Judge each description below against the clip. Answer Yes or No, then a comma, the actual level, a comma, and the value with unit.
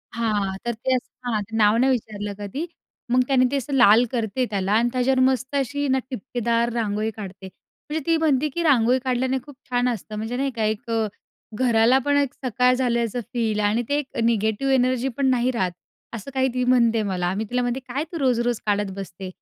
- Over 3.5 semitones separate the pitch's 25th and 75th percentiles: No, average, 3.2 semitones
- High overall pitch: Yes, high, 245 Hz